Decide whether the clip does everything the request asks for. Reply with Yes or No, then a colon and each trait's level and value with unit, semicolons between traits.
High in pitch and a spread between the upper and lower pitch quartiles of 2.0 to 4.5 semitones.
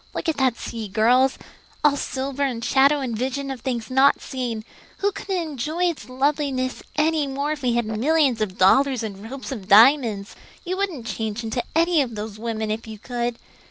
Yes: very high, 255 Hz; average, 4.1 semitones